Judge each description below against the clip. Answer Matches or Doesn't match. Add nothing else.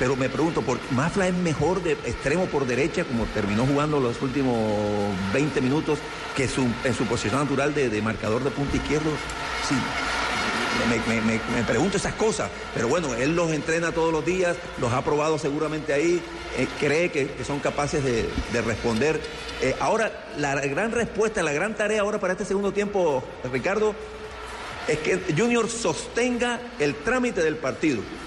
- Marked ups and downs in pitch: Matches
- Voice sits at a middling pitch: Matches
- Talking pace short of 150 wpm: Doesn't match